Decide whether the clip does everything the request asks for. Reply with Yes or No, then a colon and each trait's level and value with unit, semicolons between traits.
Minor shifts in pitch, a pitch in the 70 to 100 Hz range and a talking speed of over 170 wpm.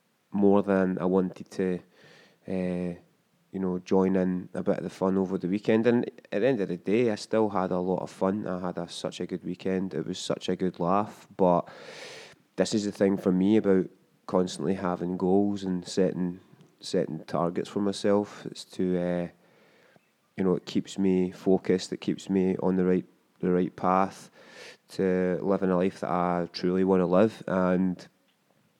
Yes: narrow, 1.1 semitones; very low, 95 Hz; average, 190 wpm